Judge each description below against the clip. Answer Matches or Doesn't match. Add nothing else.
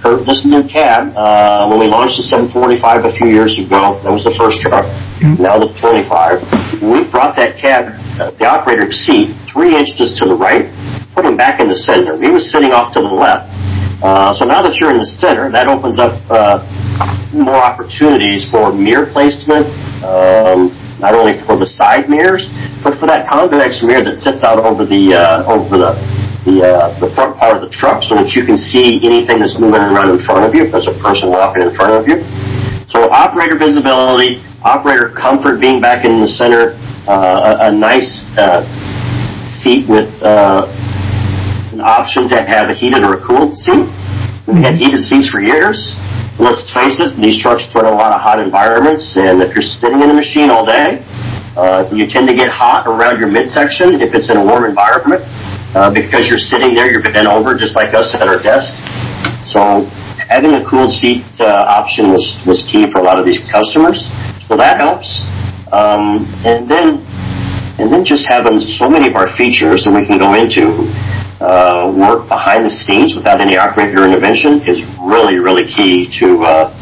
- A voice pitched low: Matches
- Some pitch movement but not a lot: Matches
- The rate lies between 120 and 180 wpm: Doesn't match